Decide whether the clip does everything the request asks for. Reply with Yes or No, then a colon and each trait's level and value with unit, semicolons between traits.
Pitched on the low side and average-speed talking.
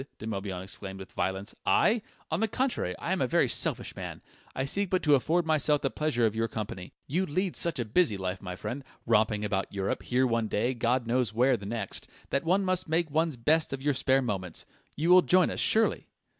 No: low, 130 Hz; fast, 220 wpm